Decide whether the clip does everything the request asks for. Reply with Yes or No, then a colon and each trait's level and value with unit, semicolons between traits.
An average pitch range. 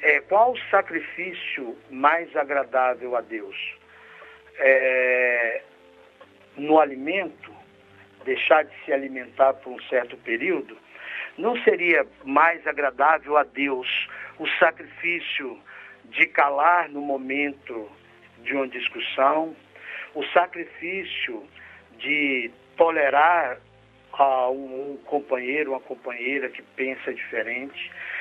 Yes: average, 4.8 semitones